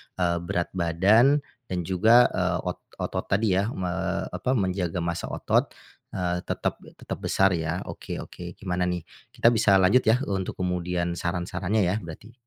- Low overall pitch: Yes, very low, 90 Hz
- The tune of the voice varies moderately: No, narrow, 2.2 semitones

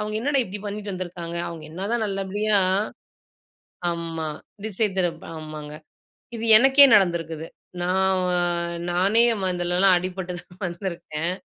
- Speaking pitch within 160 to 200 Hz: Yes, medium, 185 Hz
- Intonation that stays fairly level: No, average, 3.2 semitones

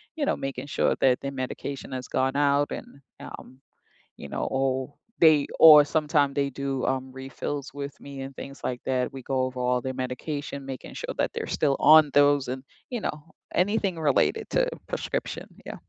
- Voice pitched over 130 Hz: Yes, medium, 140 Hz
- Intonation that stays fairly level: Yes, narrow, 1.9 semitones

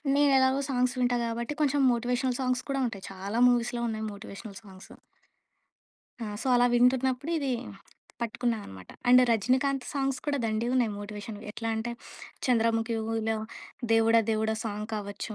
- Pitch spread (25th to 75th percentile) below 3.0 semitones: Yes, narrow, 2.6 semitones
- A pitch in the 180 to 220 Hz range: No, high, 235 Hz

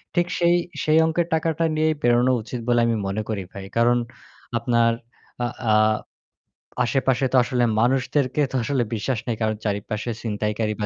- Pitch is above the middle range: No, low, 120 Hz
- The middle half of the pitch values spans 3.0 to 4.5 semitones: Yes, average, 4.1 semitones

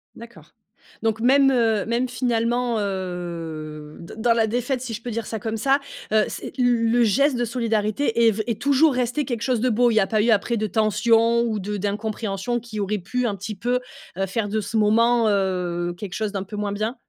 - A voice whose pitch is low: No, high, 225 Hz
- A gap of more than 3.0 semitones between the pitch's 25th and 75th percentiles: No, average, 2.7 semitones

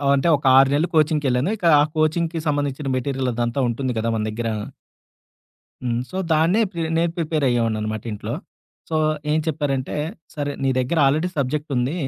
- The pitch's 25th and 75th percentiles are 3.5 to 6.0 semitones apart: Yes, average, 4.0 semitones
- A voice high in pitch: No, medium, 140 Hz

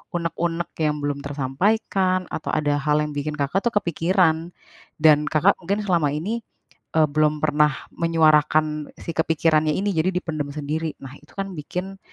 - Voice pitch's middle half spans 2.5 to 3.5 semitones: Yes, average, 2.9 semitones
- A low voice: No, medium, 155 Hz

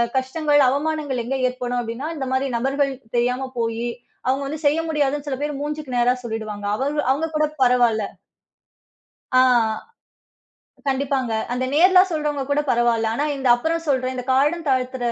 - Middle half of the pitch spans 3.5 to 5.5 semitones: No, average, 3.0 semitones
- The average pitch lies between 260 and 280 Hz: Yes, very high, 265 Hz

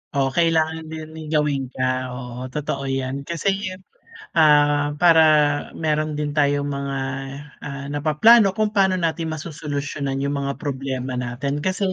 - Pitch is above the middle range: No, medium, 145 Hz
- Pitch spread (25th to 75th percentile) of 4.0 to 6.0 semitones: No, average, 2.7 semitones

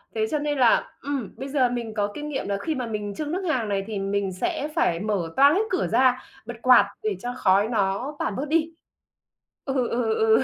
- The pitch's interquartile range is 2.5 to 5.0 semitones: No, wide, 5.5 semitones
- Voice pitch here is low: No, high, 240 Hz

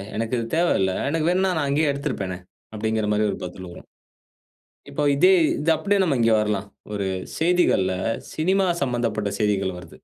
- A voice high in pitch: No, low, 115 Hz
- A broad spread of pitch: Yes, wide, 7.8 semitones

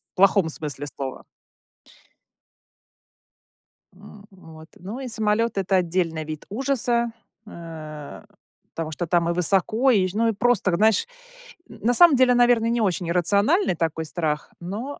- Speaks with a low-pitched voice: No, high, 190 Hz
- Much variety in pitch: Yes, wide, 5.9 semitones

